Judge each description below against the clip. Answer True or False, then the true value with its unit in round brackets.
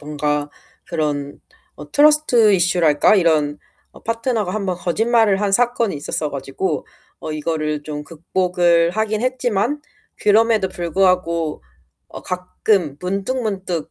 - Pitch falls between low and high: True (180 Hz)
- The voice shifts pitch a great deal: True (5.7 semitones)